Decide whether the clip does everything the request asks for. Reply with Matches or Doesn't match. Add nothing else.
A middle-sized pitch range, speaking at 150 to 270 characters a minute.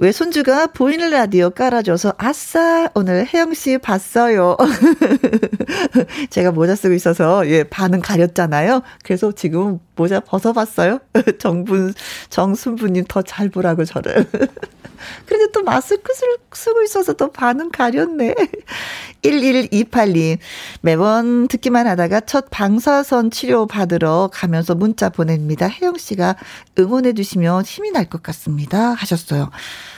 Doesn't match